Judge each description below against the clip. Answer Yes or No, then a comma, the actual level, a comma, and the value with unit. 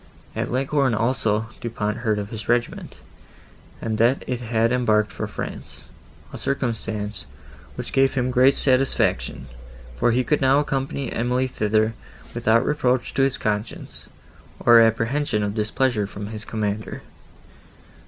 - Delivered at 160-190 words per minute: No, average, 140 wpm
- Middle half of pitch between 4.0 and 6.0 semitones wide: No, average, 3.2 semitones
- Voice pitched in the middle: No, low, 115 Hz